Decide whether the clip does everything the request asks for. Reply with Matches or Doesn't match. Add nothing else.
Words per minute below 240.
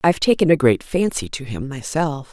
Matches